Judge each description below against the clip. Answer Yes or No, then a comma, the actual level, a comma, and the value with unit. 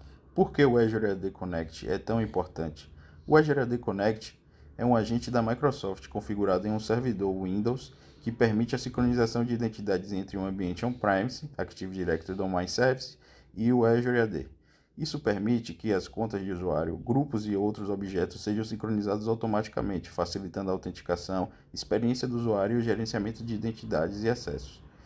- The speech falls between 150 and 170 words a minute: Yes, average, 160 wpm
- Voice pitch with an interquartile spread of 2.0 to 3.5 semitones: No, average, 3.9 semitones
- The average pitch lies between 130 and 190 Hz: No, low, 105 Hz